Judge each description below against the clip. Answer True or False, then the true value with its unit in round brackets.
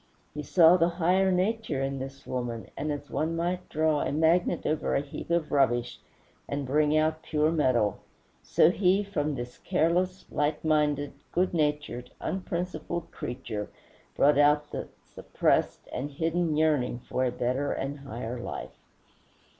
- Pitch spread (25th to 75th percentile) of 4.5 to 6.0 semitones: False (3.8 semitones)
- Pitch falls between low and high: True (150 Hz)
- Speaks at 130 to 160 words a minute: True (150 wpm)